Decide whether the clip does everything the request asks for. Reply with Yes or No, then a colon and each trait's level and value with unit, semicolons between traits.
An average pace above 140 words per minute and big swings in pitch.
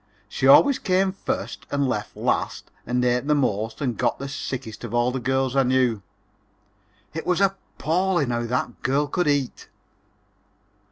No: average, 160 wpm; average, 3.7 semitones